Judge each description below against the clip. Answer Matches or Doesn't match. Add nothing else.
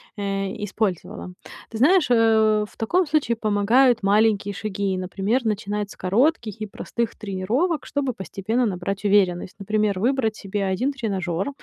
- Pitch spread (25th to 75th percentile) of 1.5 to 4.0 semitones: Matches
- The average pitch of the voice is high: Matches